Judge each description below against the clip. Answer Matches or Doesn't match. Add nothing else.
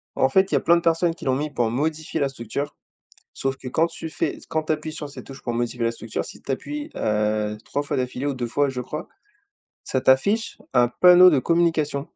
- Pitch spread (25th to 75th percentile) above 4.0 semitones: Matches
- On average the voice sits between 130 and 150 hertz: Matches